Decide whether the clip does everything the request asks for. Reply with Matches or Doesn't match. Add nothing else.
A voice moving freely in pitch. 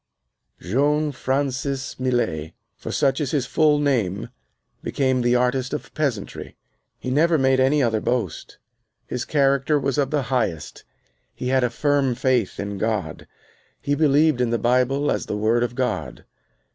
Doesn't match